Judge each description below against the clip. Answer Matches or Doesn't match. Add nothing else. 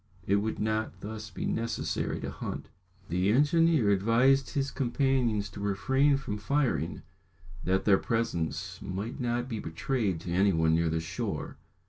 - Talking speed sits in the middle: Matches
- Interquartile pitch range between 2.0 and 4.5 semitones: Doesn't match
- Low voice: Matches